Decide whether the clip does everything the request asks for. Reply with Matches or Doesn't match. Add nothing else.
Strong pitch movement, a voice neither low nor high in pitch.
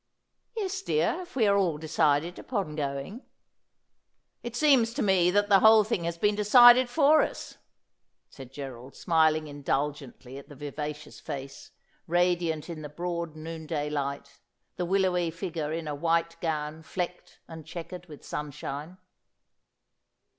Doesn't match